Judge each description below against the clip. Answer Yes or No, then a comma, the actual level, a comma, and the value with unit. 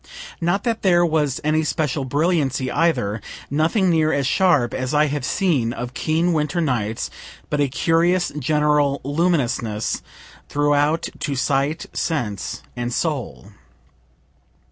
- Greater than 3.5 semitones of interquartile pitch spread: Yes, average, 4.0 semitones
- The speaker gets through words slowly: Yes, slow, 125 wpm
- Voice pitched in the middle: Yes, medium, 150 Hz